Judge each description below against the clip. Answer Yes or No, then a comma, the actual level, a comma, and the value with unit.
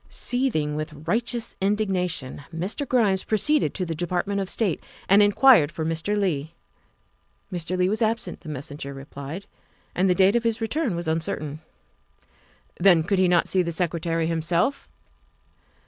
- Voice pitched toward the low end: No, medium, 180 Hz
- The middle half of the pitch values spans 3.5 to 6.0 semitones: Yes, average, 4.5 semitones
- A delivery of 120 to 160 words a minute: Yes, average, 155 wpm